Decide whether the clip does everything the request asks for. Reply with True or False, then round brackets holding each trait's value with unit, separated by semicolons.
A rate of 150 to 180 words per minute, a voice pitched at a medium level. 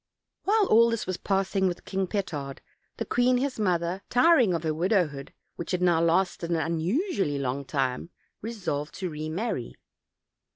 True (155 wpm; 180 Hz)